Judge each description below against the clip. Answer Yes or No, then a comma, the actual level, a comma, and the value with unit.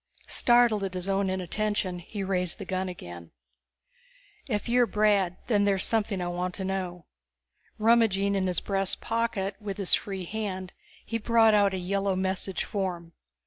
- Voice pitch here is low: No, high, 195 Hz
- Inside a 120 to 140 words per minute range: No, average, 155 wpm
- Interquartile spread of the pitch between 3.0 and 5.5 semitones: No, narrow, 2.4 semitones